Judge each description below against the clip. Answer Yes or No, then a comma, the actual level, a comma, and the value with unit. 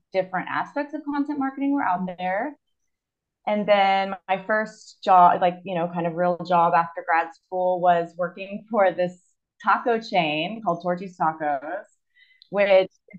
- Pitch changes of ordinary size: Yes, average, 3.1 semitones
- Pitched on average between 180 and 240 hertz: Yes, medium, 185 Hz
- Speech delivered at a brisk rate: No, average, 150 wpm